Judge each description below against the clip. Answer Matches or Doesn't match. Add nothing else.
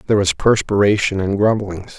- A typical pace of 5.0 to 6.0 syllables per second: Matches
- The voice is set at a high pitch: Doesn't match